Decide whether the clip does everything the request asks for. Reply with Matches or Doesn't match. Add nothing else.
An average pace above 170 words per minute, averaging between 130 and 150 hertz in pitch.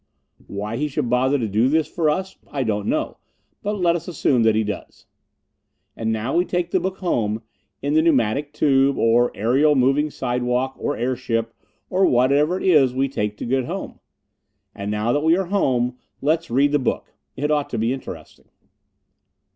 Matches